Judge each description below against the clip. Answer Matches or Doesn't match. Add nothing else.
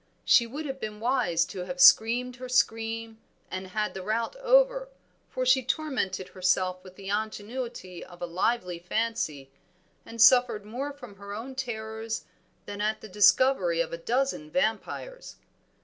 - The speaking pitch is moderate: Doesn't match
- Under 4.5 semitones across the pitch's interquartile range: Doesn't match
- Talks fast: Doesn't match